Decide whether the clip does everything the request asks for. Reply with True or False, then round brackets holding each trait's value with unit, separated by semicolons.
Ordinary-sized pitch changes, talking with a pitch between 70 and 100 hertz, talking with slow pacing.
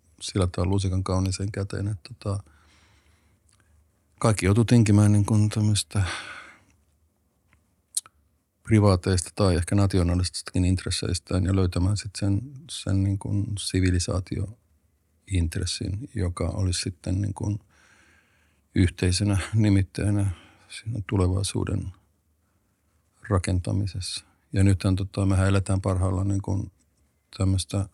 False (2.1 semitones; 95 Hz; 90 wpm)